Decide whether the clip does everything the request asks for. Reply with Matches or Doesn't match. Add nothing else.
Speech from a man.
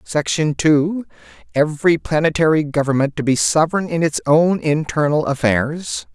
Matches